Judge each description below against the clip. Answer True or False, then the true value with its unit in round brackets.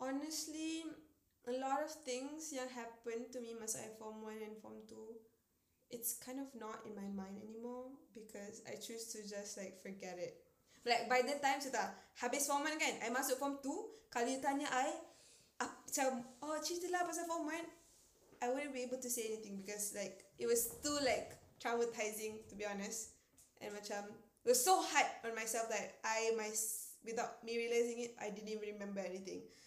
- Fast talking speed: True (185 wpm)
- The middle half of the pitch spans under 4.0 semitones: False (4.3 semitones)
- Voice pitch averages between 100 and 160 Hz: False (235 Hz)